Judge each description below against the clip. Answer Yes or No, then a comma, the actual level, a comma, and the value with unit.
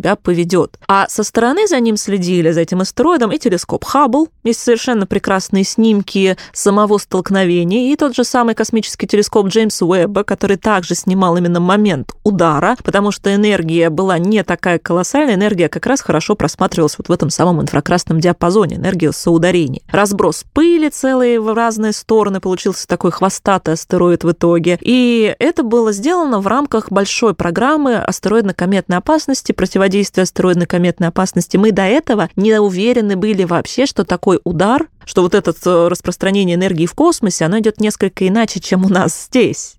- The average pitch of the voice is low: No, high, 195 Hz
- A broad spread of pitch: No, average, 3.9 semitones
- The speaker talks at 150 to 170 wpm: Yes, fast, 160 wpm